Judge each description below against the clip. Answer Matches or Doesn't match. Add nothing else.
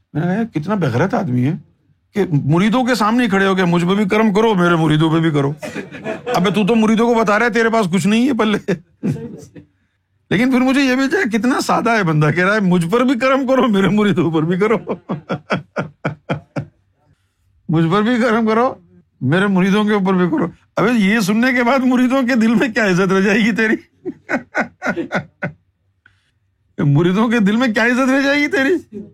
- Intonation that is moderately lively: Doesn't match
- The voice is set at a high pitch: Matches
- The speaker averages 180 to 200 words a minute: Matches